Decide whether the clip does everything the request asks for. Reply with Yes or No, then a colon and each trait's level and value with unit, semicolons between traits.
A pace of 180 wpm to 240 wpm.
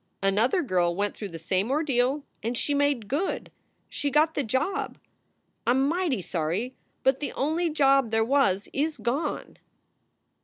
No: average, 155 wpm